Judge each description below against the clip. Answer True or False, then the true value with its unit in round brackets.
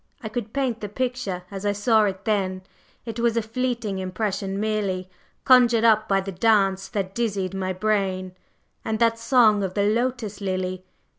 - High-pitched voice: True (210 Hz)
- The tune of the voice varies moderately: True (3.1 semitones)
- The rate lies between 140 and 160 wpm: False (170 wpm)